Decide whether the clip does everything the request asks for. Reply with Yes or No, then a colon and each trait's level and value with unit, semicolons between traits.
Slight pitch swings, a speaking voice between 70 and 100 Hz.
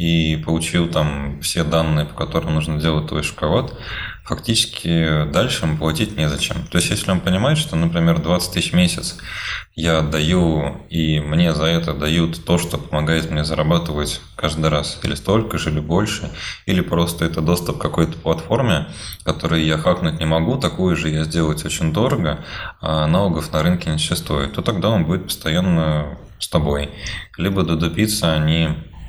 Yes: narrow, 1.7 semitones; very low, 80 Hz